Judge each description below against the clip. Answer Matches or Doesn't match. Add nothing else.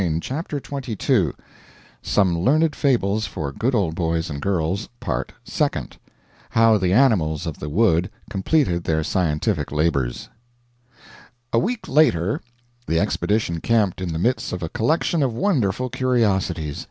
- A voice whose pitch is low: Matches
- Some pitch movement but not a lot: Doesn't match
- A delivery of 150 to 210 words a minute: Doesn't match